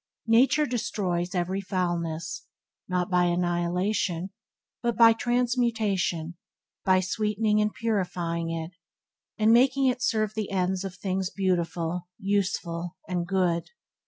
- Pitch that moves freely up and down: No, average, 3.8 semitones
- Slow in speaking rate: Yes, slow, 115 wpm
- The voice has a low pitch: No, medium, 185 Hz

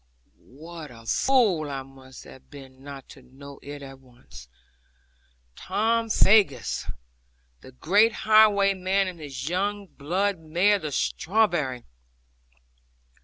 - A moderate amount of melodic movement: No, wide, 6.9 semitones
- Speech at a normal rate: No, slow, 115 wpm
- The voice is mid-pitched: Yes, medium, 155 Hz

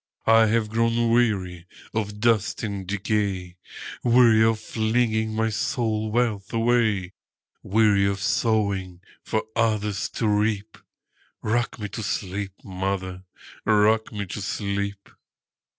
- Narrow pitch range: Yes, narrow, 2.3 semitones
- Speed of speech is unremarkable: No, slow, 105 wpm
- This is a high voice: No, low, 105 Hz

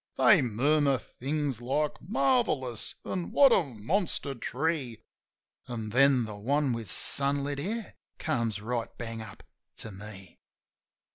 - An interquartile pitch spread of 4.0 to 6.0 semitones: Yes, average, 4.9 semitones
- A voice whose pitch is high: No, low, 135 Hz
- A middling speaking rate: No, slow, 130 wpm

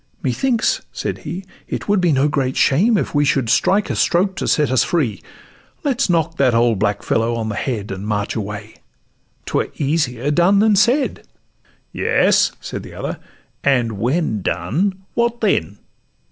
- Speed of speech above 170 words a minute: No, average, 165 wpm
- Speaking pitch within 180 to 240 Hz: No, medium, 140 Hz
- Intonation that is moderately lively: No, wide, 9.0 semitones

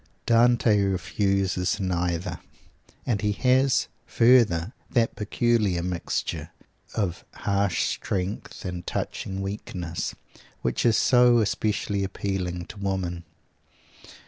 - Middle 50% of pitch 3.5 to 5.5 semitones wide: Yes, average, 3.8 semitones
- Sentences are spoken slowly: Yes, slow, 95 wpm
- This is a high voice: No, low, 100 Hz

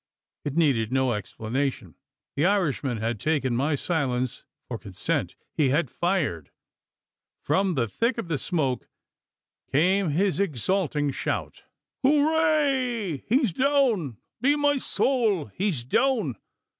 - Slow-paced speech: Yes, slow, 120 wpm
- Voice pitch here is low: No, medium, 160 Hz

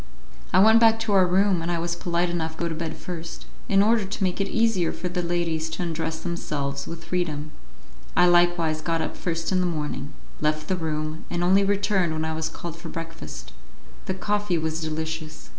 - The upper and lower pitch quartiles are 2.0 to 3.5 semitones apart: Yes, narrow, 2.5 semitones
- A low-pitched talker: No, medium, 170 Hz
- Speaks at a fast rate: Yes, fast, 210 wpm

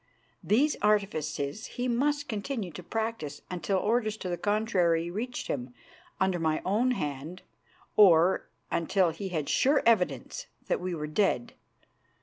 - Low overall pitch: No, high, 190 Hz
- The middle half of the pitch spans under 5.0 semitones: No, average, 5.3 semitones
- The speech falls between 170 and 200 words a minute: No, slow, 135 wpm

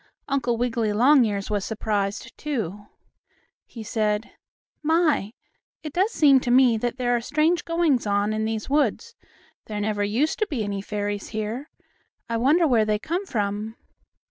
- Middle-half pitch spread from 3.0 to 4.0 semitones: No, wide, 5.4 semitones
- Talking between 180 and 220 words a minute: No, average, 155 wpm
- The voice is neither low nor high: No, high, 230 Hz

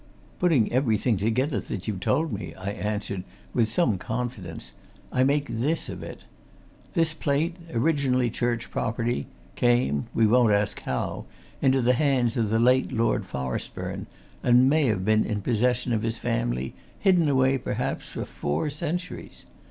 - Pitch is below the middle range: Yes, low, 120 Hz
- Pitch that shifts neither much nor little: Yes, average, 4.2 semitones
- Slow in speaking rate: No, average, 150 wpm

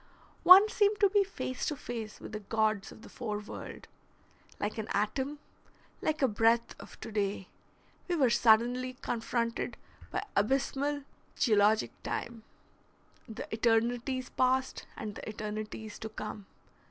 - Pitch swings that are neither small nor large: Yes, average, 3.5 semitones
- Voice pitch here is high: Yes, high, 230 Hz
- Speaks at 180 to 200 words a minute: No, average, 140 wpm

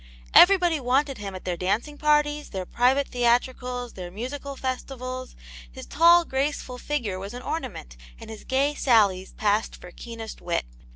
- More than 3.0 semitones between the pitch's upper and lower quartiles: Yes, wide, 5.5 semitones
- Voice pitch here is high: Yes, very high, 250 Hz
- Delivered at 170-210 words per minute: No, average, 155 wpm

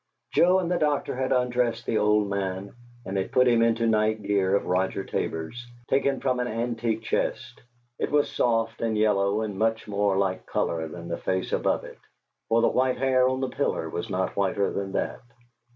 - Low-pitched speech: Yes, low, 110 Hz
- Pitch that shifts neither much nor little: Yes, average, 3.9 semitones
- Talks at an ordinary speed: Yes, average, 195 wpm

